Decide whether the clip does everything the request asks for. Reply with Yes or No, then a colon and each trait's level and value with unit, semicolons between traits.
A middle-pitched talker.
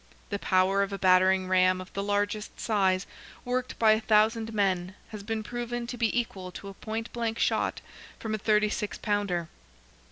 No: high, 205 Hz